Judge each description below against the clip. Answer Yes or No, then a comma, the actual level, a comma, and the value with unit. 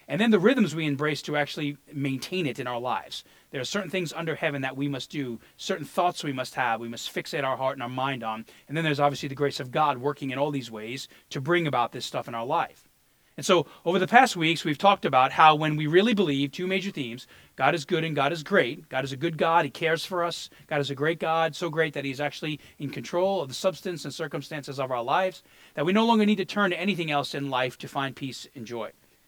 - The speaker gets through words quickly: Yes, fast, 260 wpm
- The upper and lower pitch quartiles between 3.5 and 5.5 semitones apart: Yes, average, 4.1 semitones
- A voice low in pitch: No, medium, 150 Hz